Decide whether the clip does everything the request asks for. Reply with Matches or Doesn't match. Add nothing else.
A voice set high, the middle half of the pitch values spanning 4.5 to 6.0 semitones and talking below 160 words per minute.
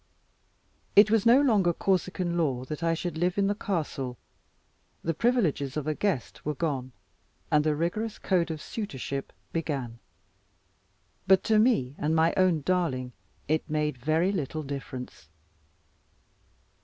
Doesn't match